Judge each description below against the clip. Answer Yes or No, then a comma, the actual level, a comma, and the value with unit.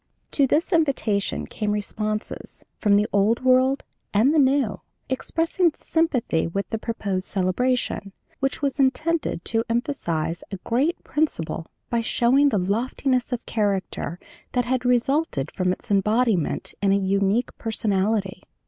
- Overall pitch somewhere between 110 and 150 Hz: No, high, 230 Hz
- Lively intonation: No, average, 4.9 semitones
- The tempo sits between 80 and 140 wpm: Yes, slow, 135 wpm